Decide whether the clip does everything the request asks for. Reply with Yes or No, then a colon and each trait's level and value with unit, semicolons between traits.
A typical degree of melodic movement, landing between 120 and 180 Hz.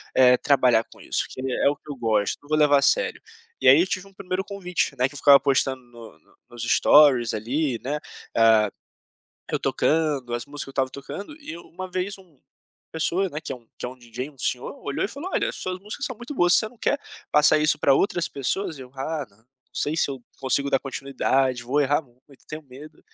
Yes: average, 4.9 semitones; medium, 140 Hz